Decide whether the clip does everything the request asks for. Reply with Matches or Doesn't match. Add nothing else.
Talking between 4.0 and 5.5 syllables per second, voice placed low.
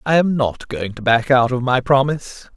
Matches